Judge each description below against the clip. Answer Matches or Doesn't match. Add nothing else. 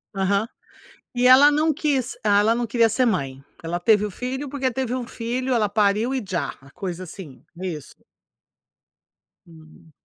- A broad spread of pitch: Matches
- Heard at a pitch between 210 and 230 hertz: Matches